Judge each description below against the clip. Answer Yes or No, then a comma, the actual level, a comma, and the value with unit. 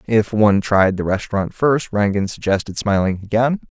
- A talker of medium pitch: No, low, 105 Hz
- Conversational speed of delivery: Yes, average, 160 wpm